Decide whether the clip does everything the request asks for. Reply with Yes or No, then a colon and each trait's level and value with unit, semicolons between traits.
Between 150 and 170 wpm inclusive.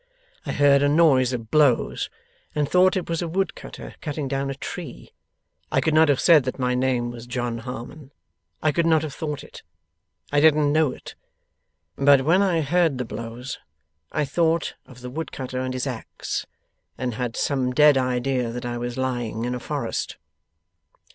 No: average, 185 wpm